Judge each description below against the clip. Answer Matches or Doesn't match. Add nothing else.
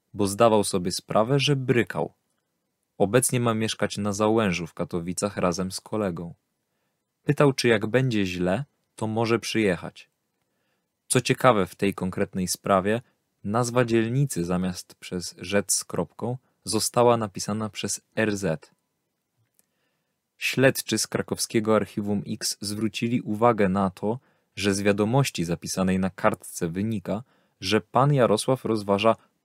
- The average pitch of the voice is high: Doesn't match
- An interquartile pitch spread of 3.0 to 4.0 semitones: Matches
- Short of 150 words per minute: Matches